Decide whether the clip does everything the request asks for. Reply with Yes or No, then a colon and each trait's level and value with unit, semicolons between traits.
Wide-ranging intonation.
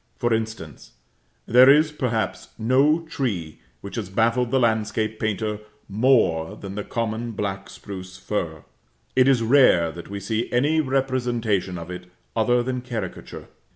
No: average, 4.2 semitones